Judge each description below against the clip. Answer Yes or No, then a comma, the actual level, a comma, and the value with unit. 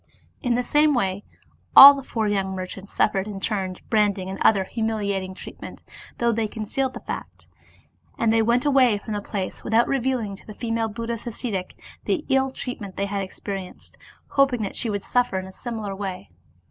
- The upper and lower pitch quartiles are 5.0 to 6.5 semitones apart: No, average, 3.7 semitones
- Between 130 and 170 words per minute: No, average, 185 wpm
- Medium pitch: No, high, 215 Hz